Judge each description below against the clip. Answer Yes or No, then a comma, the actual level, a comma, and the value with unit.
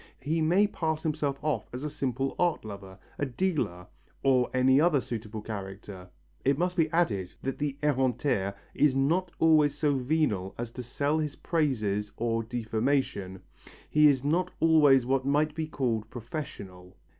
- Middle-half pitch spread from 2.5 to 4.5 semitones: No, wide, 5.4 semitones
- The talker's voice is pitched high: No, low, 135 Hz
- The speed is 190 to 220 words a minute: No, average, 155 wpm